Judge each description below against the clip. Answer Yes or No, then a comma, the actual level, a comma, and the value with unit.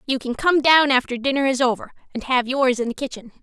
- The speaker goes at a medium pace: No, fast, 245 wpm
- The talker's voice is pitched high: Yes, very high, 260 Hz